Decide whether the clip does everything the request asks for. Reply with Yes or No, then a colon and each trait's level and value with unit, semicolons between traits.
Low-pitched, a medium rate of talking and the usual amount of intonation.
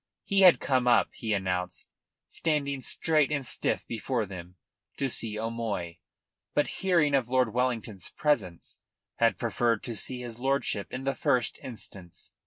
Yes: low, 120 Hz; average, 150 wpm; average, 4.3 semitones